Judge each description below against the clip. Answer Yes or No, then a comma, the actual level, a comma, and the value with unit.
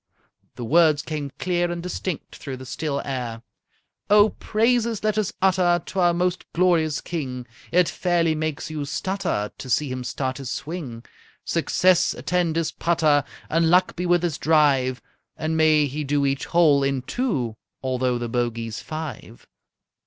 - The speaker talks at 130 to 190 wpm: Yes, average, 160 wpm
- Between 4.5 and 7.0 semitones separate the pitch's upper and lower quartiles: Yes, average, 4.8 semitones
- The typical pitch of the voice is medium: Yes, medium, 155 Hz